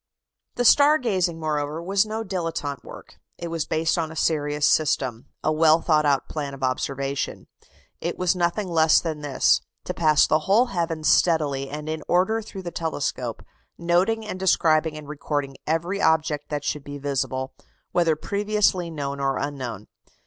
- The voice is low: No, medium, 160 Hz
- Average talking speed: Yes, average, 165 wpm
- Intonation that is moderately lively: Yes, average, 3.4 semitones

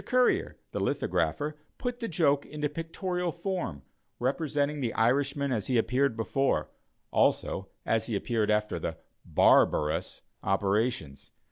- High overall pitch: No, medium, 140 Hz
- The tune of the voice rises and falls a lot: Yes, wide, 5.7 semitones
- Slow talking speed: Yes, slow, 130 wpm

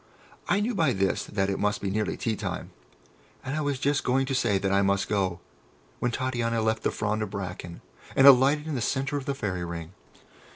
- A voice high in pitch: No, low, 110 Hz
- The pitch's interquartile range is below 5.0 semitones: No, wide, 5.5 semitones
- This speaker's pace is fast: Yes, fast, 215 wpm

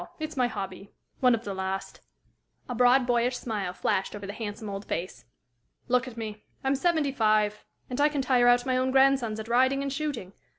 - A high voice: Yes, high, 245 Hz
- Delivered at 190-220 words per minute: Yes, average, 200 wpm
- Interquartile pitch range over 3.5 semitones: Yes, average, 4.2 semitones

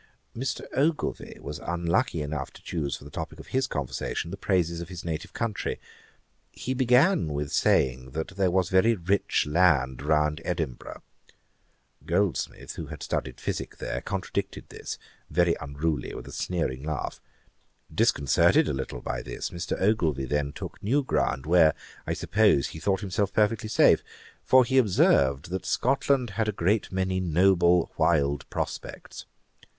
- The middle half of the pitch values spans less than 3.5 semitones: No, wide, 5.4 semitones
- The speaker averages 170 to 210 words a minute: No, average, 155 wpm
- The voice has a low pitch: Yes, very low, 85 Hz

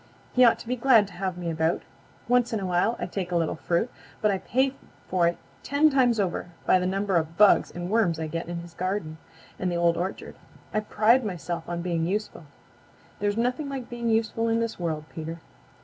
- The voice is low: No, high, 190 Hz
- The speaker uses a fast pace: Yes, fast, 215 wpm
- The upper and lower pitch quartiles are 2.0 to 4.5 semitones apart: No, average, 5.1 semitones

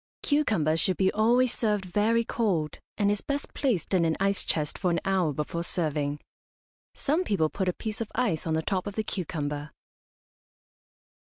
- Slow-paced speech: No, average, 175 wpm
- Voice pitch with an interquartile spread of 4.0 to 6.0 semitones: Yes, average, 5.3 semitones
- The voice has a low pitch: No, high, 190 Hz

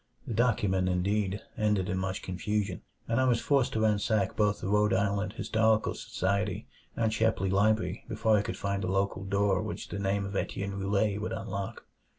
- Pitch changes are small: Yes, narrow, 1.9 semitones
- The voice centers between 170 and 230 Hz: No, low, 100 Hz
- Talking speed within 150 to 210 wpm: Yes, average, 180 wpm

